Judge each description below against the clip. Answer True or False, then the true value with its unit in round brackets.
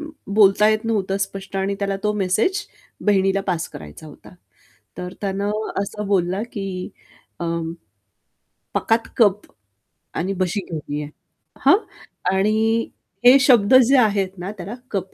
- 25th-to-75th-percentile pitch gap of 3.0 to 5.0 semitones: False (2.6 semitones)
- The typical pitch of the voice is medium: False (200 Hz)